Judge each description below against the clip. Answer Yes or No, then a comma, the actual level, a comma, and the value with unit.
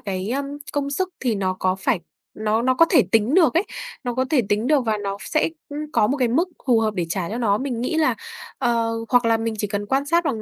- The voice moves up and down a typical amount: Yes, average, 4.9 semitones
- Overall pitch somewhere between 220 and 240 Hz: Yes, high, 235 Hz